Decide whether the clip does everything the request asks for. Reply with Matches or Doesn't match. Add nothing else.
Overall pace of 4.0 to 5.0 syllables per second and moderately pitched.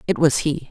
Doesn't match